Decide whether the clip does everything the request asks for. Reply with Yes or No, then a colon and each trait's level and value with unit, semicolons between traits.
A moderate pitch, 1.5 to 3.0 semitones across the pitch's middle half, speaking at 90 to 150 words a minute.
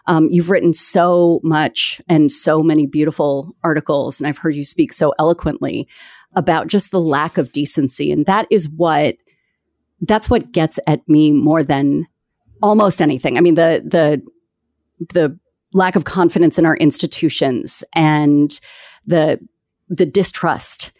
Yes: medium, 160 Hz; average, 2.7 semitones; average, 145 wpm